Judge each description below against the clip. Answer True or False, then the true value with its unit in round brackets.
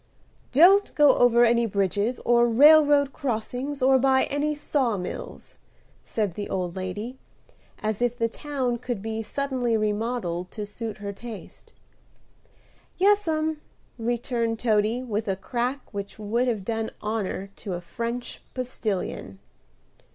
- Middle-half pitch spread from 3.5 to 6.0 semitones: True (3.9 semitones)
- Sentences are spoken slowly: True (130 wpm)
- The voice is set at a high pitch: True (235 Hz)